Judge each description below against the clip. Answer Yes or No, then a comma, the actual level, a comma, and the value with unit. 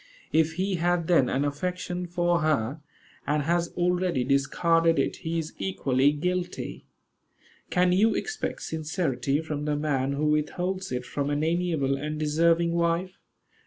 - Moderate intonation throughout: Yes, average, 3.3 semitones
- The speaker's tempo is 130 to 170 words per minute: Yes, average, 145 wpm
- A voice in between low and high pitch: Yes, medium, 165 Hz